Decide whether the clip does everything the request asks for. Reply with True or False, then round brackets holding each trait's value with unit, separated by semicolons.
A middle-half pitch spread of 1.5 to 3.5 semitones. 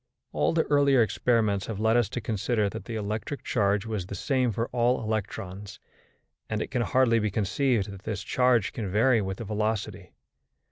True (3.1 semitones)